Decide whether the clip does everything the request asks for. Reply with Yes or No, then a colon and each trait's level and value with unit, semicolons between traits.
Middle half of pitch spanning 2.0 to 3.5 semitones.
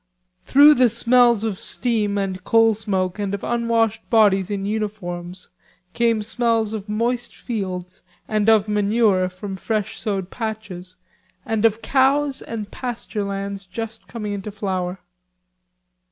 Yes: average, 2.8 semitones